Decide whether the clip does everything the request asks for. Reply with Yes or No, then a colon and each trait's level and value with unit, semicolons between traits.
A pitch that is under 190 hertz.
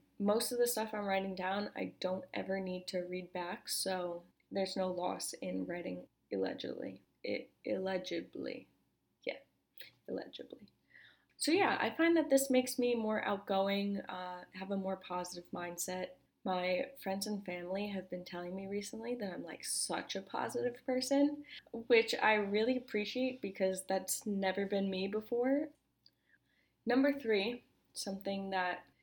No: high, 195 Hz